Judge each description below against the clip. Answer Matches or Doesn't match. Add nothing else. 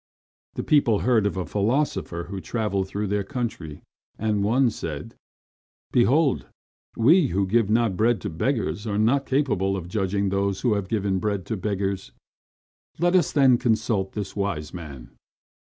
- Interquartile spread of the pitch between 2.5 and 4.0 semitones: Matches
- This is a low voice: Matches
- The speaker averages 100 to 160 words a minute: Matches